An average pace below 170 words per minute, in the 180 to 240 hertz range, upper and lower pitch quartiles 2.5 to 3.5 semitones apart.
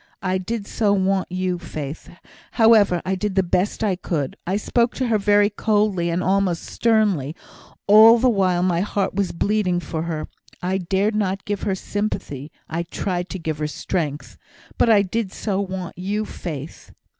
No: average, 175 wpm; high, 190 Hz; average, 2.9 semitones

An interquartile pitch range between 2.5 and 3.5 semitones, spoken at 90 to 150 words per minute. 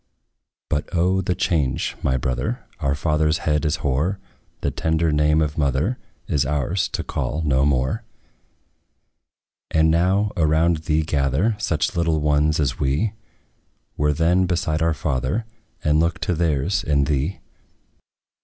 Yes: average, 2.8 semitones; average, 140 wpm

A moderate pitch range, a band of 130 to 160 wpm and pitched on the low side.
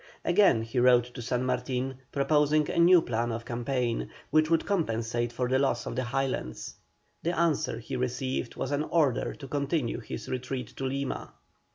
No: average, 3.3 semitones; average, 175 wpm; low, 130 Hz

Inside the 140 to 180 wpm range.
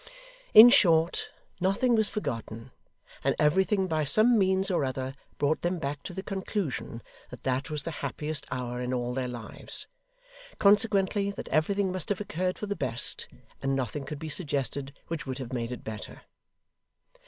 Yes: average, 165 wpm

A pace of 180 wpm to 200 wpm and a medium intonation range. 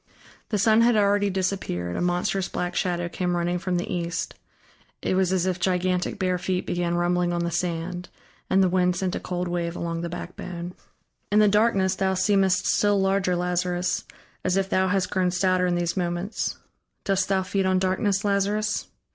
No: average, 185 wpm; narrow, 1.6 semitones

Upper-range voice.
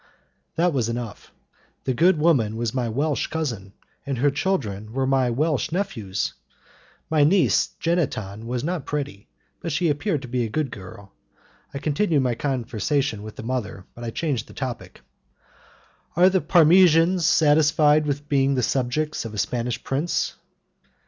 No: medium, 140 Hz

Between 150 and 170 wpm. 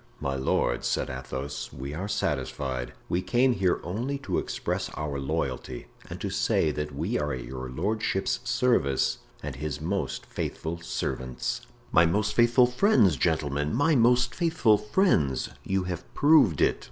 Yes: average, 155 wpm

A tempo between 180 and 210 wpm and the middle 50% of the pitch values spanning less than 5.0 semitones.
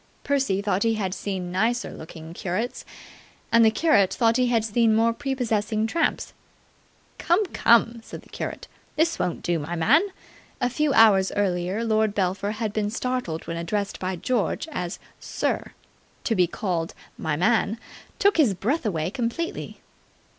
No: average, 155 wpm; average, 4.6 semitones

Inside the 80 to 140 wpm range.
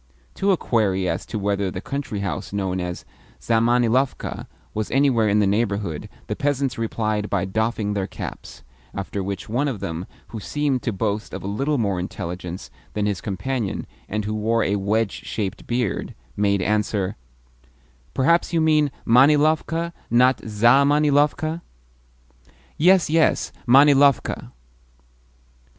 Yes: slow, 135 wpm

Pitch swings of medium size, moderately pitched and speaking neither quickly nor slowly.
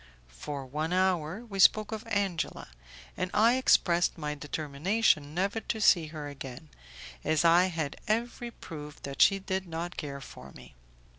Yes: average, 5.0 semitones; medium, 170 Hz; average, 155 wpm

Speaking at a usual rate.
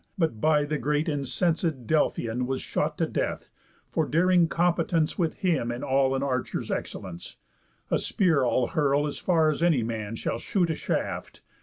Yes: average, 170 wpm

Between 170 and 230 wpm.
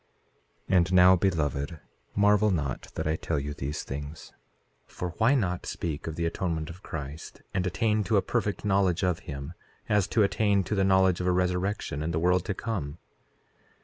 Yes: average, 185 wpm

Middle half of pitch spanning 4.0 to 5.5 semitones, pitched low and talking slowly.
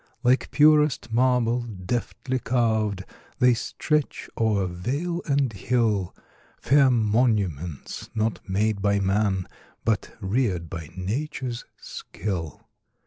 Yes: average, 4.7 semitones; low, 110 Hz; slow, 100 wpm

